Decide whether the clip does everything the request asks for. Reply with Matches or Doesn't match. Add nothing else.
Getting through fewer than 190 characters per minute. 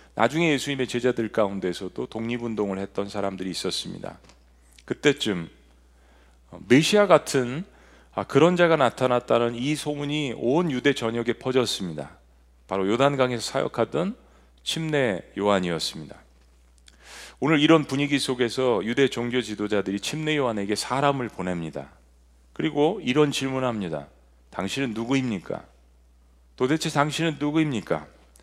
Doesn't match